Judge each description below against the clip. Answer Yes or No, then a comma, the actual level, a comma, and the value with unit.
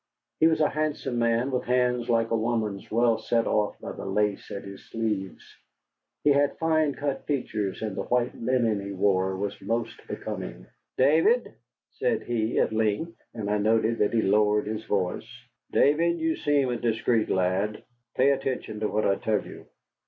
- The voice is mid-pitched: No, low, 115 Hz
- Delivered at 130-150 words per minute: No, average, 175 wpm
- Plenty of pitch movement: No, average, 3.9 semitones